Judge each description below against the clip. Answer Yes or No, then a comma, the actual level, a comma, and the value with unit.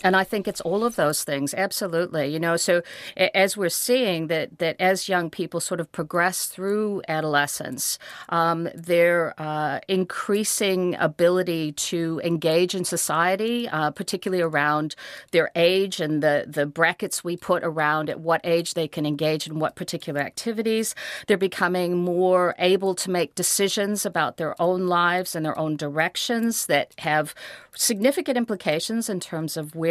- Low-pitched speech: No, medium, 175 Hz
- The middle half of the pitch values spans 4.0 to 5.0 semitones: No, average, 3.3 semitones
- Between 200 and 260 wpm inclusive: No, average, 160 wpm